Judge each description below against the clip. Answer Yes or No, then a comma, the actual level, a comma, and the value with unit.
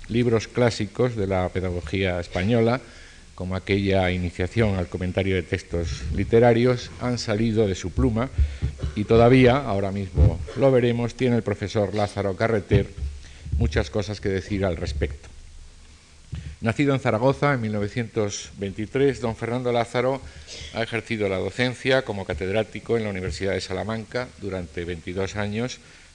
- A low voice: Yes, low, 100 Hz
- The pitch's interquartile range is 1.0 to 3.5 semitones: No, average, 4.3 semitones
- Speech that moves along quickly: No, average, 135 wpm